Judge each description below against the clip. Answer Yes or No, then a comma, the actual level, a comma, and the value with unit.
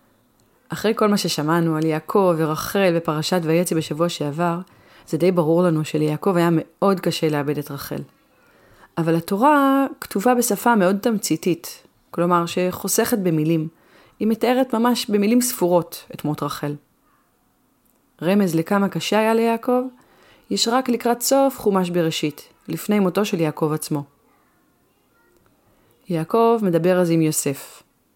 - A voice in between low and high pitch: Yes, medium, 180 Hz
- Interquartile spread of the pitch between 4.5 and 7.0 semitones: Yes, average, 5.0 semitones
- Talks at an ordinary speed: Yes, average, 130 wpm